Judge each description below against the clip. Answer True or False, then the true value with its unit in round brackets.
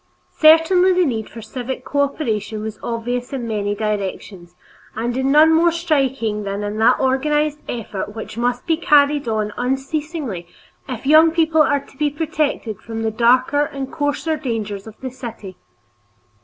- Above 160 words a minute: False (155 wpm)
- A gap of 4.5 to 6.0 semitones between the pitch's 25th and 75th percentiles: True (5.4 semitones)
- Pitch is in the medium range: False (255 Hz)